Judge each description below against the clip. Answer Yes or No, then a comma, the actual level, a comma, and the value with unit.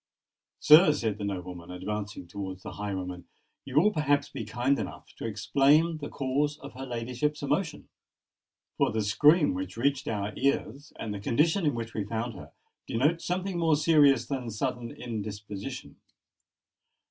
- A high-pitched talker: No, low, 125 Hz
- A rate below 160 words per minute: Yes, average, 150 wpm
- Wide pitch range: Yes, wide, 6.1 semitones